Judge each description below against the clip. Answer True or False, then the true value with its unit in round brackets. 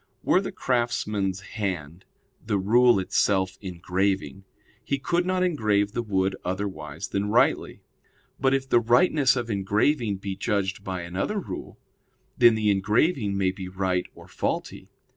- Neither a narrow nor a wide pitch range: True (4.1 semitones)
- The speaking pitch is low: True (100 Hz)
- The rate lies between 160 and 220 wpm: False (140 wpm)